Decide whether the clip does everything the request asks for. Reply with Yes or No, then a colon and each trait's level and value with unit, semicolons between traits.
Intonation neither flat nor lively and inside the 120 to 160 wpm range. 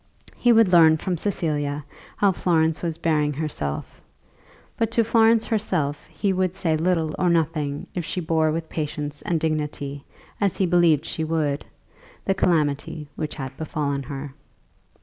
Yes: average, 3.5 semitones; average, 150 wpm